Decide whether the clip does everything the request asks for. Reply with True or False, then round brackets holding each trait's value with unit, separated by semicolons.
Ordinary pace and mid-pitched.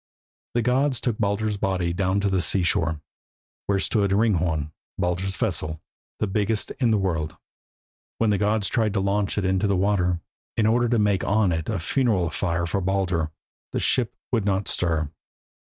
False (175 wpm; 100 Hz)